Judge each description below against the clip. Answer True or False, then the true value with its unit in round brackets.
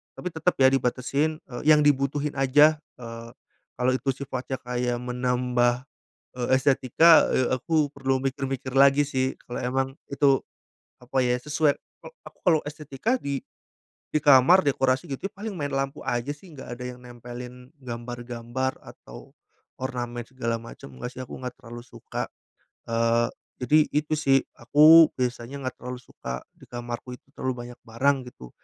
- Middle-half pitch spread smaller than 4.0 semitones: True (2.5 semitones)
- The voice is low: True (130 Hz)